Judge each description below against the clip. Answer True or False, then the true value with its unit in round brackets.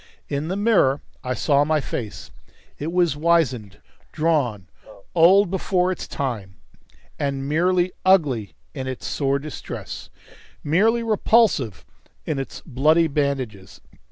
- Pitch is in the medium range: True (150 Hz)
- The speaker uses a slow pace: True (120 wpm)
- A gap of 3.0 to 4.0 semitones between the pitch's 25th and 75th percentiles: False (5.2 semitones)